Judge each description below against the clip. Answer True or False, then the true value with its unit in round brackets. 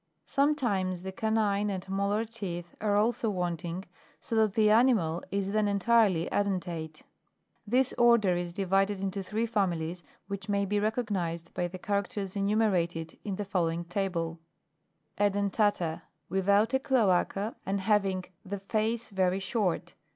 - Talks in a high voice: True (200 Hz)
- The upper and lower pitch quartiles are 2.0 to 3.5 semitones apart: True (2.8 semitones)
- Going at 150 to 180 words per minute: False (135 wpm)